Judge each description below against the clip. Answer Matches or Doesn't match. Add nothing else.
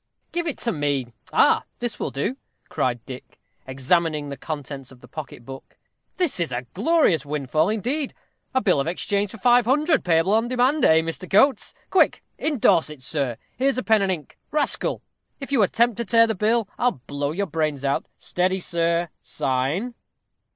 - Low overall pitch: Doesn't match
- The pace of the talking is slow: Doesn't match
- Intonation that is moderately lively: Doesn't match